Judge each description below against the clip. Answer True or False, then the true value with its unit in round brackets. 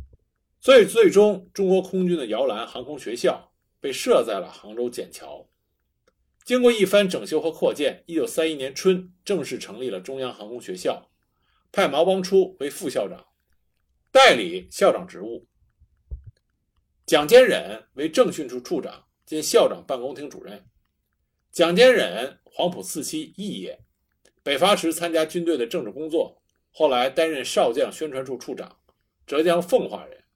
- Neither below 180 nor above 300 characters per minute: True (225 characters per minute)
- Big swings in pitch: False (4.7 semitones)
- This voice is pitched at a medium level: True (180 Hz)